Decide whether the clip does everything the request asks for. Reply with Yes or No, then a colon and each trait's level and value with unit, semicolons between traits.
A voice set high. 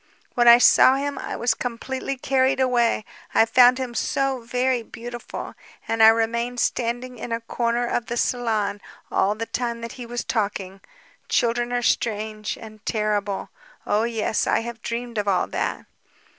Yes: high, 235 Hz